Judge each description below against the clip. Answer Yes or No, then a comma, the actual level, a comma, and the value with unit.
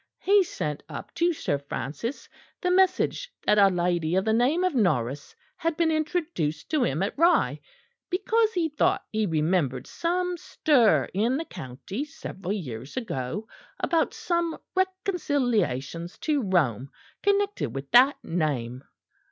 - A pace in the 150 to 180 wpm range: No, average, 140 wpm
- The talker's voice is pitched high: Yes, high, 220 Hz